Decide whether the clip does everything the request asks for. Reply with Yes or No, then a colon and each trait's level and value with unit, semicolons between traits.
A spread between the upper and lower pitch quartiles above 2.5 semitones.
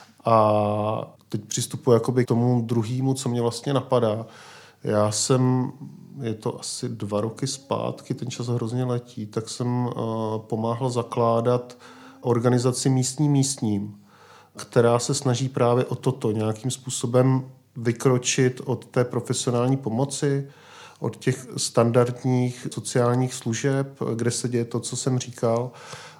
No: narrow, 2.0 semitones